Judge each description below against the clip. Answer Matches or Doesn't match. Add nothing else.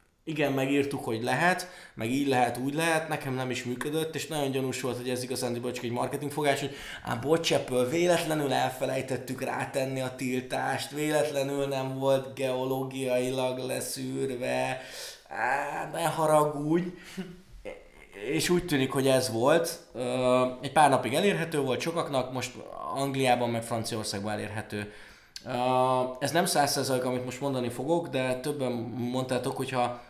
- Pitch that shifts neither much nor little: Matches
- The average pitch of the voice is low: Matches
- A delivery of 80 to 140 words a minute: Matches